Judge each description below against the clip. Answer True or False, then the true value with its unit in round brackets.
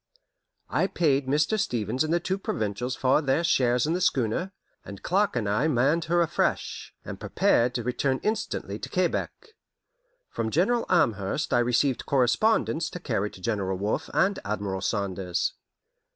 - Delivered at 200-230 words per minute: False (155 wpm)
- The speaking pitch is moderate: False (130 Hz)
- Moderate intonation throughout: False (7.8 semitones)